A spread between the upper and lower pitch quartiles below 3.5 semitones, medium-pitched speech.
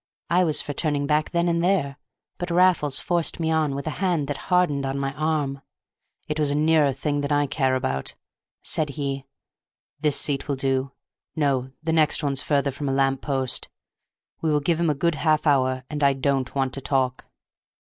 Yes: narrow, 2.5 semitones; medium, 145 Hz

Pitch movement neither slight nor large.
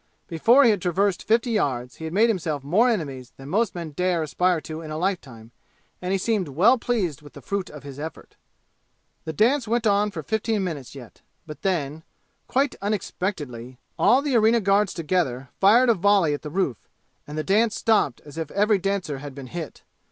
No: wide, 6.1 semitones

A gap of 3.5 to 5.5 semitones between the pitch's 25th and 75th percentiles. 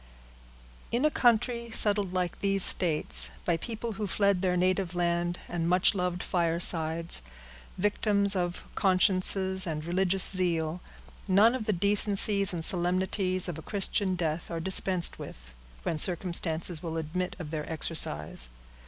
No: average, 2.7 semitones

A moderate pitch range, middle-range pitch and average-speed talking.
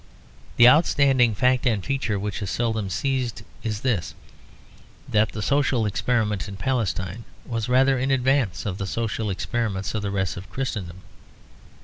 No: average, 4.3 semitones; low, 110 Hz; average, 150 wpm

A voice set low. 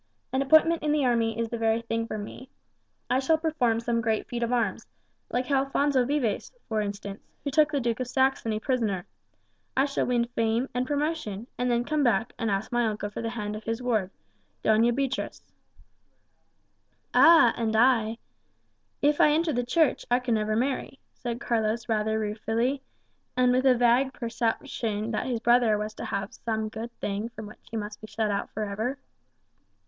No: high, 235 Hz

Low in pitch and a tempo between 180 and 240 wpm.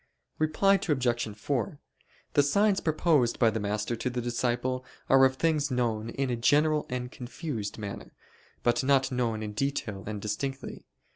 No: low, 125 Hz; average, 155 wpm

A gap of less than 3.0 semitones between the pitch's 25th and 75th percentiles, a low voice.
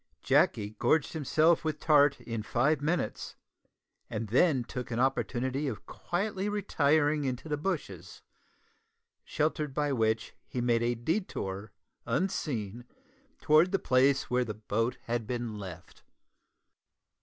No: average, 5.0 semitones; low, 130 Hz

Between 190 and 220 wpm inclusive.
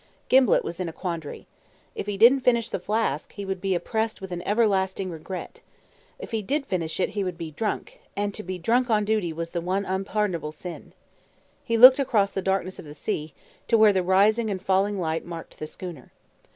Yes: fast, 205 wpm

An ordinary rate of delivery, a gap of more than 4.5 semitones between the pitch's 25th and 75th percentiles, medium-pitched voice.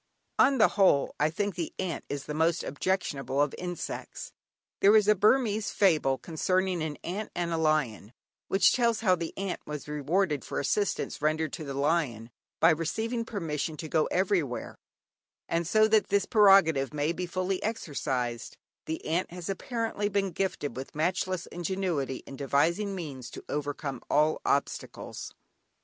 Yes: average, 160 wpm; average, 4.9 semitones; medium, 170 Hz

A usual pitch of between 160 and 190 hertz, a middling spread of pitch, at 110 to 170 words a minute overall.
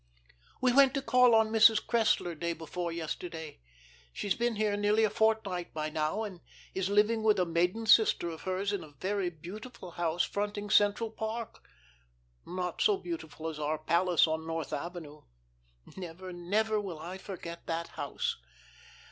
Yes: medium, 185 Hz; average, 4.5 semitones; average, 160 wpm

